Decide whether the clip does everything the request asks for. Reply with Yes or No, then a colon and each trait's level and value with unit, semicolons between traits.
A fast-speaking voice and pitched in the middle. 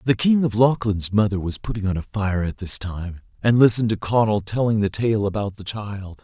No: fast, 220 wpm; low, 105 Hz